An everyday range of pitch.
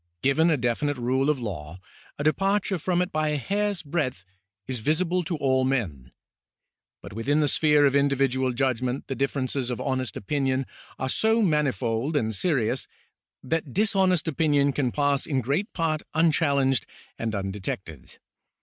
Yes: average, 3.8 semitones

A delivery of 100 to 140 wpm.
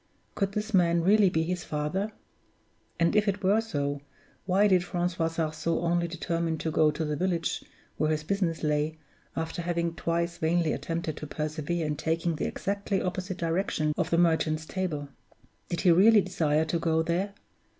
No: average, 170 wpm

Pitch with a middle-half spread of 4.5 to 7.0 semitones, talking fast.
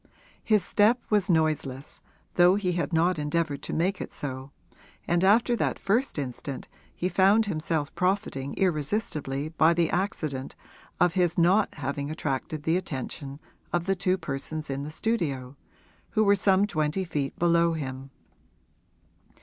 No: average, 4.8 semitones; average, 145 wpm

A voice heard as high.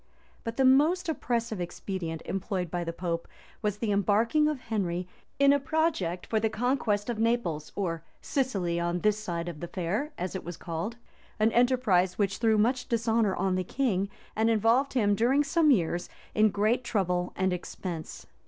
Yes: high, 210 Hz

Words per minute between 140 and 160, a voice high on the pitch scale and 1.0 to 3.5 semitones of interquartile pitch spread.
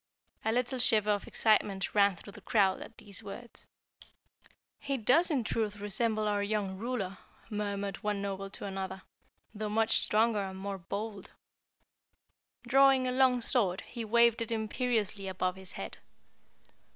Yes: average, 150 wpm; high, 210 Hz; average, 2.9 semitones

